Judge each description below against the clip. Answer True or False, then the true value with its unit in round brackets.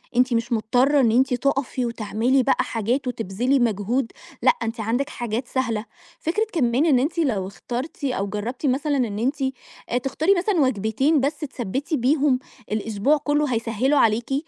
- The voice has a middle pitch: False (250 Hz)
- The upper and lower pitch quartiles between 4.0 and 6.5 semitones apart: False (3.6 semitones)